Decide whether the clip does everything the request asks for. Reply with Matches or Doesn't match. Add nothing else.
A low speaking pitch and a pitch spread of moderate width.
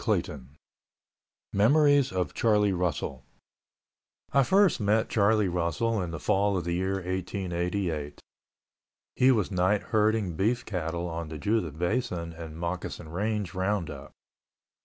Matches